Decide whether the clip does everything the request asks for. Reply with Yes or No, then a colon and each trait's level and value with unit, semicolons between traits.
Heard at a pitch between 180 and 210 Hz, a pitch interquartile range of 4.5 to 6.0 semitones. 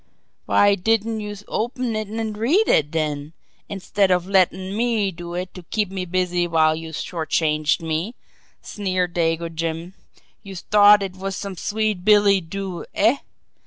No: high, 190 Hz; average, 3.6 semitones